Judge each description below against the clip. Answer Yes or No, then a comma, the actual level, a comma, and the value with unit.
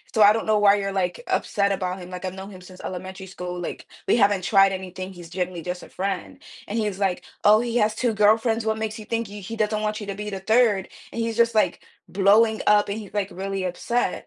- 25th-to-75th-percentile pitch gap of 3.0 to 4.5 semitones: No, narrow, 2.5 semitones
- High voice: Yes, high, 200 Hz